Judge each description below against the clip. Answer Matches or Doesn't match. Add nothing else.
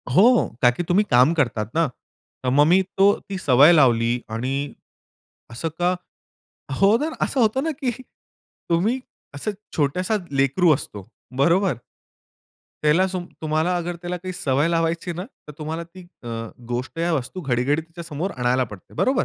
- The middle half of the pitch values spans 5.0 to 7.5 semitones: Matches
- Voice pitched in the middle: Matches